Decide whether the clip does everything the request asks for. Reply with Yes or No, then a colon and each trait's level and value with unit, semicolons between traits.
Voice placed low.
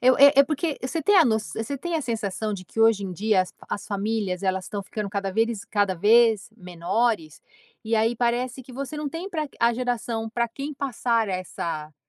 No: high, 225 Hz